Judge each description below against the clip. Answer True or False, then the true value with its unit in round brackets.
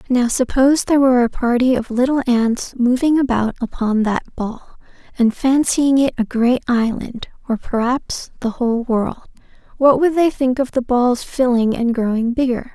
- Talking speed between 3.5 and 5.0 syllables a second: True (4.8 syllables/s)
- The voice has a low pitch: False (250 Hz)